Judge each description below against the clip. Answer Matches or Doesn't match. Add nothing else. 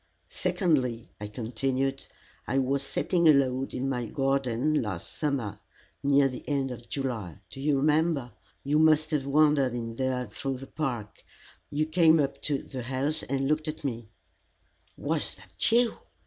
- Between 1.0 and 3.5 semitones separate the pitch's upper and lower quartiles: Matches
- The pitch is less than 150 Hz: Matches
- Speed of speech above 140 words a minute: Matches